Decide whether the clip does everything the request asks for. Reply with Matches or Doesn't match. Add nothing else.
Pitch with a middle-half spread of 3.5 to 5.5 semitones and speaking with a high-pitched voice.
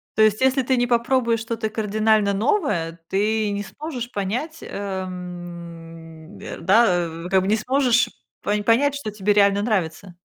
Matches